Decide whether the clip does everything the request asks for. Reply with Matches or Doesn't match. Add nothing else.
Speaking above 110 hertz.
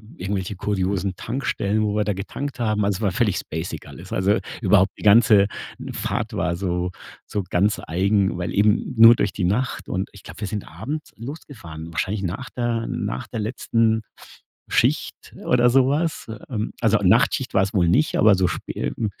Doesn't match